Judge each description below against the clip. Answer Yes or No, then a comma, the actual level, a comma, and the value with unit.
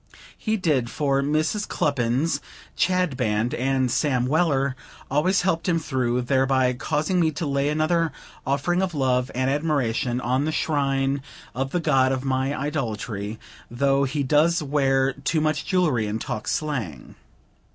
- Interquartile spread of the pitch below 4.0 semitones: Yes, average, 3.3 semitones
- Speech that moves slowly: No, average, 145 wpm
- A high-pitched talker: No, medium, 140 Hz